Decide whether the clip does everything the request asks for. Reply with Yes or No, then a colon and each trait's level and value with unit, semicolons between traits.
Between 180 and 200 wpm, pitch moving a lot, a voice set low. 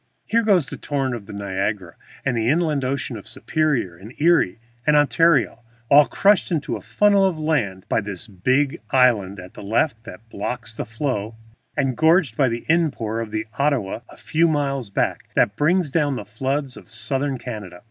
Yes: average, 185 wpm; wide, 5.8 semitones; low, 130 Hz